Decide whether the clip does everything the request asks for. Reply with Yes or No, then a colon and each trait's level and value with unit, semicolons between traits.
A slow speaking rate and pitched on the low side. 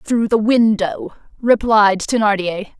No: slow, 105 wpm; high, 215 Hz